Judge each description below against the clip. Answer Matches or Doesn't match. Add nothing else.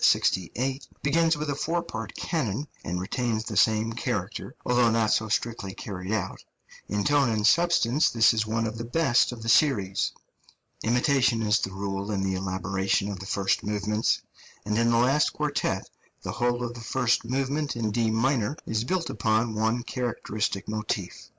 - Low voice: Matches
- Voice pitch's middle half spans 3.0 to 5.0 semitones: Matches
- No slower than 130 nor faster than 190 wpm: Matches